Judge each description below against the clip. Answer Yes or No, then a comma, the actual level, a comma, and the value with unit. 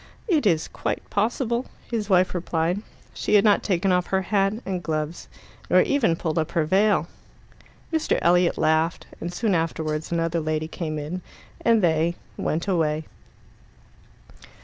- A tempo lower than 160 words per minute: Yes, average, 150 wpm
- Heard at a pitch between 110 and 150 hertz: No, medium, 175 Hz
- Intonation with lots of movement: No, average, 3.8 semitones